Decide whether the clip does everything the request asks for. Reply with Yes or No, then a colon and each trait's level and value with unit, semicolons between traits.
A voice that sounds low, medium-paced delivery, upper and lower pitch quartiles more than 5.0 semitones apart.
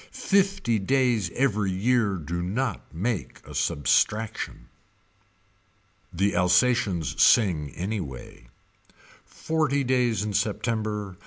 No: low, 105 Hz; slow, 85 wpm; wide, 5.4 semitones